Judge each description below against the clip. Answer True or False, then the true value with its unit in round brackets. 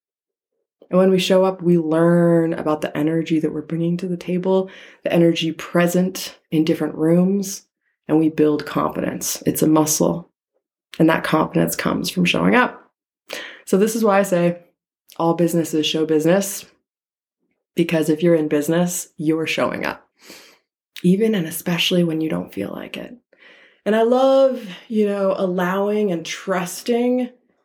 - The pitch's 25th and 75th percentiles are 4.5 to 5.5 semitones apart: False (3.4 semitones)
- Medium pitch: True (175 Hz)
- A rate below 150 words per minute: False (155 wpm)